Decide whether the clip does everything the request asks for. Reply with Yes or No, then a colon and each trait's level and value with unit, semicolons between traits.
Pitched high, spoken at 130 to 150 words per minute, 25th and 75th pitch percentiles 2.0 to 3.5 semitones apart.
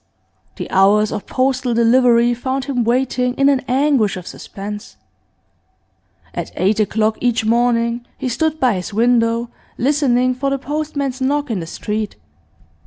Yes: high, 245 Hz; average, 145 wpm; average, 3.2 semitones